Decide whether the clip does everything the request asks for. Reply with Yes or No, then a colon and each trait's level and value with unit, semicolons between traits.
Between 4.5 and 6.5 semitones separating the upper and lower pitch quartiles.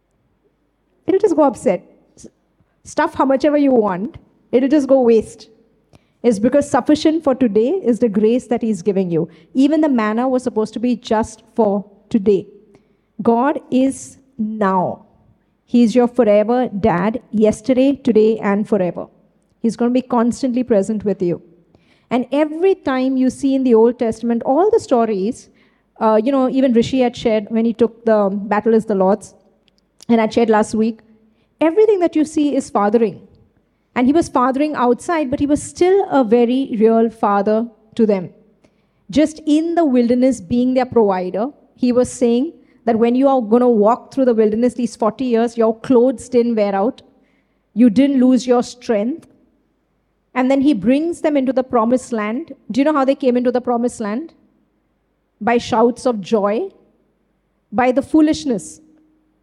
No: average, 3.5 semitones